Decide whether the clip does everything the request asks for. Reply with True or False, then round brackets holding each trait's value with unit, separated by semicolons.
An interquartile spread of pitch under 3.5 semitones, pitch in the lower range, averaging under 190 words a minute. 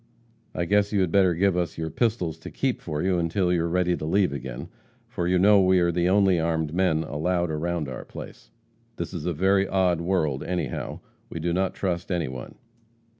False (2.6 semitones; 85 Hz; 205 wpm)